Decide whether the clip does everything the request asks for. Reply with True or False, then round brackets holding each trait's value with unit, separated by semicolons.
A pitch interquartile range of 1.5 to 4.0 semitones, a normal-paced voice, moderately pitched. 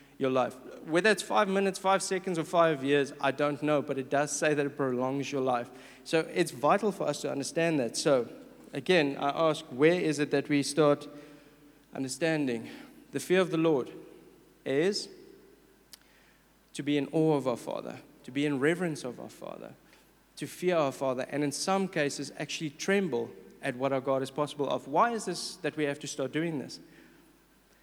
False (2.9 semitones; 195 wpm; 145 Hz)